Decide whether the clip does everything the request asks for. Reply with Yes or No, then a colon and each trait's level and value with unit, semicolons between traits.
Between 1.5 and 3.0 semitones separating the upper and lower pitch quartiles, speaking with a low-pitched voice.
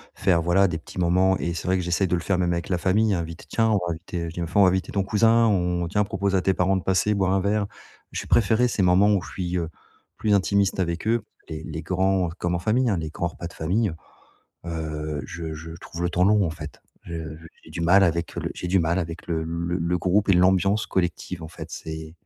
Yes: narrow, 2.5 semitones; very low, 90 Hz